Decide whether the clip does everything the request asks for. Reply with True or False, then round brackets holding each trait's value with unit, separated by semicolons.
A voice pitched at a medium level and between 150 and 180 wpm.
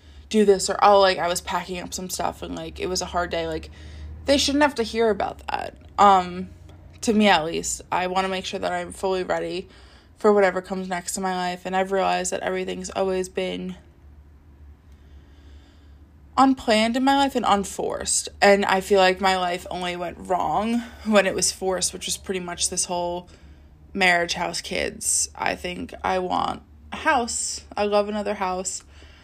False (180 Hz; 190 wpm)